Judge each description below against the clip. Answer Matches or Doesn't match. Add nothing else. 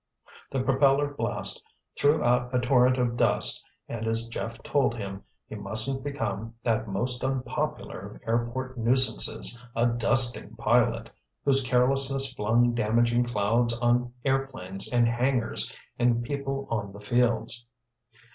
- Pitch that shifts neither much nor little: Doesn't match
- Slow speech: Matches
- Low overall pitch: Matches